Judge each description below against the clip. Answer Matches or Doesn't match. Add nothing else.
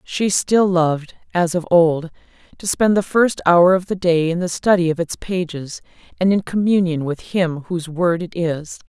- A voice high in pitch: Doesn't match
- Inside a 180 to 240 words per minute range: Matches